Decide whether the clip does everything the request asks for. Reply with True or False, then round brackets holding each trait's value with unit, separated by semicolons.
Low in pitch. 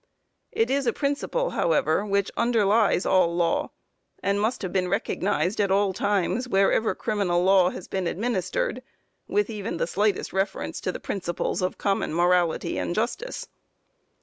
False (195 Hz)